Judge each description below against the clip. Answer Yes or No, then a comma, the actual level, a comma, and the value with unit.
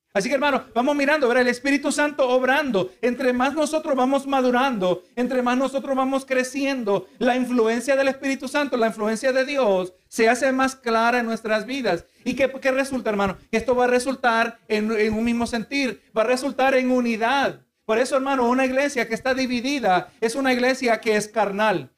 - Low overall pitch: No, very high, 250 Hz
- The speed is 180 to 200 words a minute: Yes, fast, 190 wpm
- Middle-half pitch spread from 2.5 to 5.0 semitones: Yes, average, 3.0 semitones